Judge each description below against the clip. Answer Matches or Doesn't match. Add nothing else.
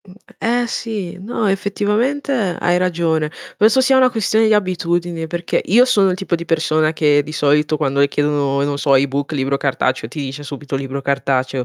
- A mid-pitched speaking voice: Matches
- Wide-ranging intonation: Matches